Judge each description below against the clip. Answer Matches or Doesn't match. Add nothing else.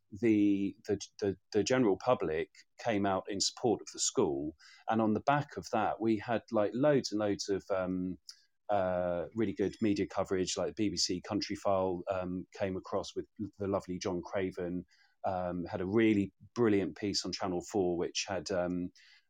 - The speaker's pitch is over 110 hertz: Doesn't match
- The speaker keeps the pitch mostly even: Doesn't match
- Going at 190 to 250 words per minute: Doesn't match